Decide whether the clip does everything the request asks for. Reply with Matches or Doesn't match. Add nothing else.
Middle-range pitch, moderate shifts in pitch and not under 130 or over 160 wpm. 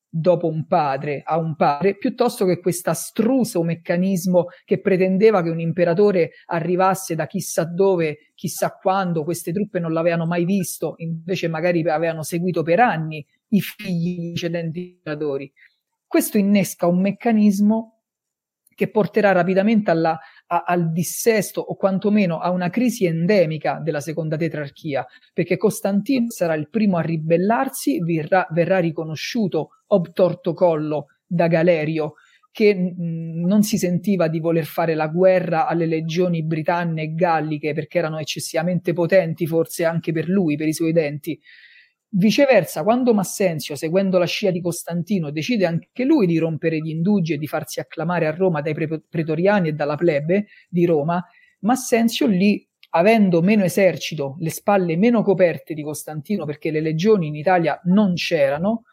Matches